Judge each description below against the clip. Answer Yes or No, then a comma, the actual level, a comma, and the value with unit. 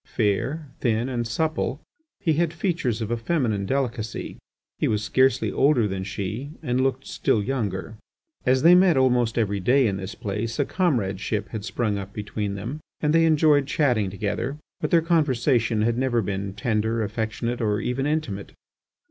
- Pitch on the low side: Yes, low, 120 Hz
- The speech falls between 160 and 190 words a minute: Yes, average, 165 wpm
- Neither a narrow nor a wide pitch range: Yes, average, 4.9 semitones